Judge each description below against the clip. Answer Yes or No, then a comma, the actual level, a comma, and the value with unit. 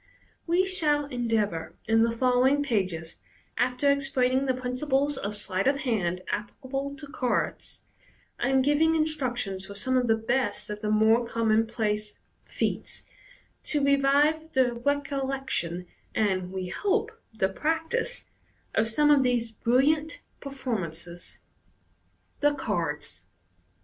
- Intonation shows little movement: No, average, 5.0 semitones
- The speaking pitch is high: Yes, very high, 250 Hz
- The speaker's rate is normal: No, slow, 130 wpm